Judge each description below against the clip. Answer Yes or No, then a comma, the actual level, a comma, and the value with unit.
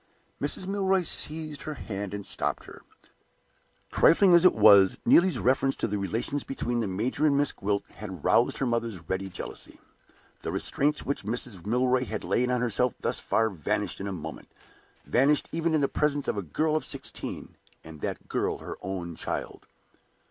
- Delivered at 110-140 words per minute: No, average, 175 wpm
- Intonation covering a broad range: Yes, wide, 6.7 semitones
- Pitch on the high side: No, low, 120 Hz